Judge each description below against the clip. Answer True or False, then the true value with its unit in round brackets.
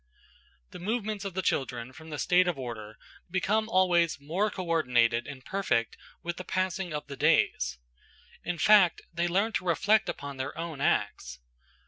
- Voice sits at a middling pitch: True (170 Hz)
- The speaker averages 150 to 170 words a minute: True (165 wpm)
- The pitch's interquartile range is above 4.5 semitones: True (5.2 semitones)